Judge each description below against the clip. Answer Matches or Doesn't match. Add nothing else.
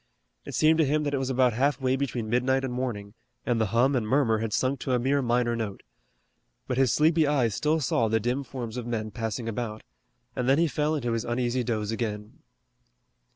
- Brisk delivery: Matches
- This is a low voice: Matches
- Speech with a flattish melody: Doesn't match